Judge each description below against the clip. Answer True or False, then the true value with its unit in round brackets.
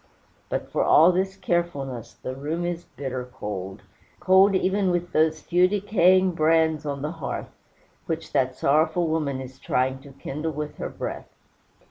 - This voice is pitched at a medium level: True (155 Hz)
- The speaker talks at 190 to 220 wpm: False (155 wpm)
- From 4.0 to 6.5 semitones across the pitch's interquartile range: True (4.5 semitones)